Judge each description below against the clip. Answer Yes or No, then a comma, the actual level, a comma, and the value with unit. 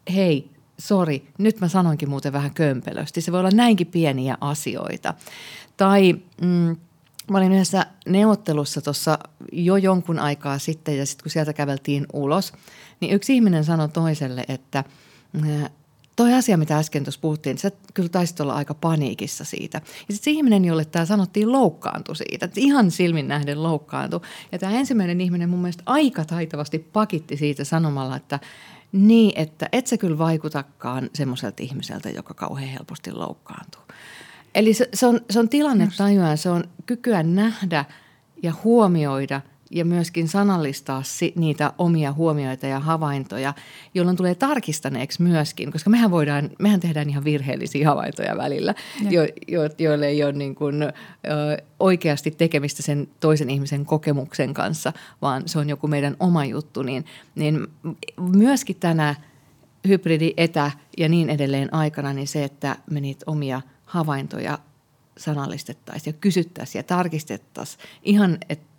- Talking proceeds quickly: No, average, 145 wpm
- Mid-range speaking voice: Yes, medium, 155 Hz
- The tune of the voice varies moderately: Yes, average, 4.2 semitones